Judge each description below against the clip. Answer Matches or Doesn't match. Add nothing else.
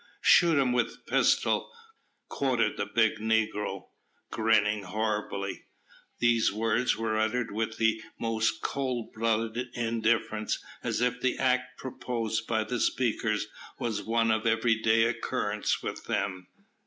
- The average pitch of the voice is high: Doesn't match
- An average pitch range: Doesn't match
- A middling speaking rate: Doesn't match